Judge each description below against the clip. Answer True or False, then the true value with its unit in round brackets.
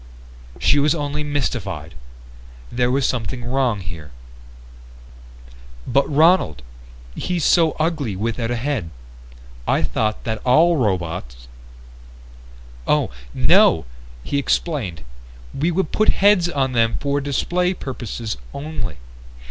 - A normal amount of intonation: False (7.8 semitones)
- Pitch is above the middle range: False (125 Hz)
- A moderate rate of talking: False (115 wpm)